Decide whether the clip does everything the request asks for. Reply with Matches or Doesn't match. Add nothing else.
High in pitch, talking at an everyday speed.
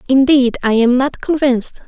Matches